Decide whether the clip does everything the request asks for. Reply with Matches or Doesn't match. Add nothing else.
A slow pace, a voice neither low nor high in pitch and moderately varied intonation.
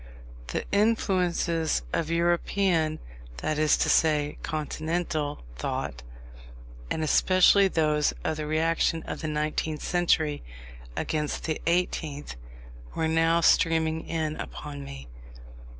Doesn't match